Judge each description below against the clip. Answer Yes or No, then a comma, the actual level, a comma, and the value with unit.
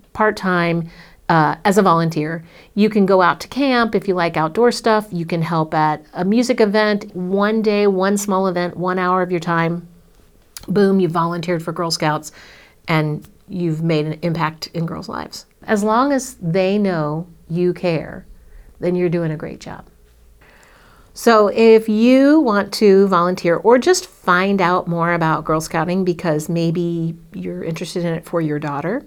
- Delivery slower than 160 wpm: No, average, 175 wpm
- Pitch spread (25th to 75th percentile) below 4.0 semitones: Yes, average, 3.5 semitones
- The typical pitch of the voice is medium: Yes, medium, 175 Hz